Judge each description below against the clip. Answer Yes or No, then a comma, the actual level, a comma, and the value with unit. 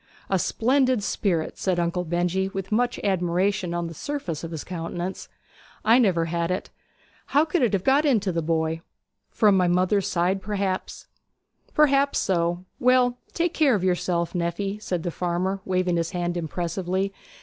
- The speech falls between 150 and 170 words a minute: Yes, average, 160 wpm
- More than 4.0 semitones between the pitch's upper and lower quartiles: No, average, 3.4 semitones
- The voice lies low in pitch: No, medium, 185 Hz